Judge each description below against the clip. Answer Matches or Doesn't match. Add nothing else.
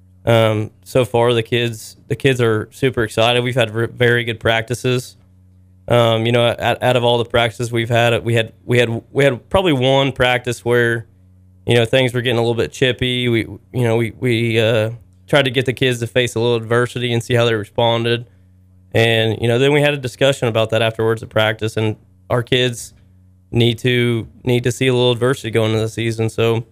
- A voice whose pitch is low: Matches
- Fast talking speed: Matches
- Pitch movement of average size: Doesn't match